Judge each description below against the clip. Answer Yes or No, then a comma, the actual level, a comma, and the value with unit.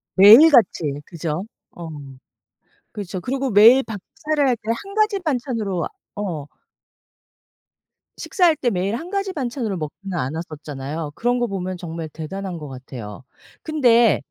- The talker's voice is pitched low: No, high, 200 Hz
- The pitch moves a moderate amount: No, wide, 7.7 semitones